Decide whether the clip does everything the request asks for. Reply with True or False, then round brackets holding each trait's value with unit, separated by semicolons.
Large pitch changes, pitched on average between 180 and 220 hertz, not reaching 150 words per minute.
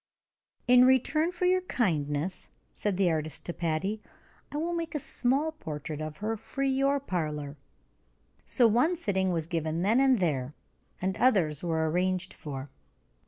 False (8.9 semitones; 190 Hz; 155 wpm)